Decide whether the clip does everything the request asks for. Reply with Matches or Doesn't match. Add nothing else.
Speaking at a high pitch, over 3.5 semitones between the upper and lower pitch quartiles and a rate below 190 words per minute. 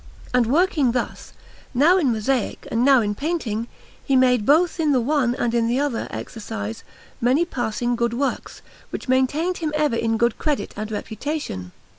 Matches